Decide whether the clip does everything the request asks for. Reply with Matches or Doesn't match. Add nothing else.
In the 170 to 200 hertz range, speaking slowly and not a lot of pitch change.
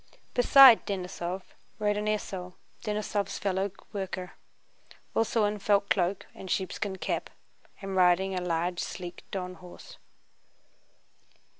Matches